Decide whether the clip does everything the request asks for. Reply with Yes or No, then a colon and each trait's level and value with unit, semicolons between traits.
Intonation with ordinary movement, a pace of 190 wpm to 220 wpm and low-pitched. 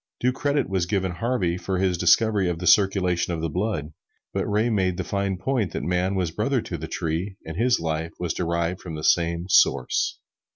Yes: average, 3.3 semitones; fast, 205 wpm; very low, 90 Hz